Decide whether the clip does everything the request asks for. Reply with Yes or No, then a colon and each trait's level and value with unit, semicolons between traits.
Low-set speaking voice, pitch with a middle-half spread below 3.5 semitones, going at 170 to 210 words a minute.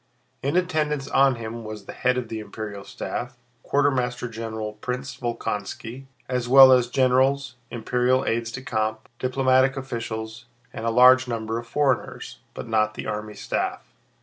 No: low, 125 Hz; average, 2.8 semitones; average, 150 wpm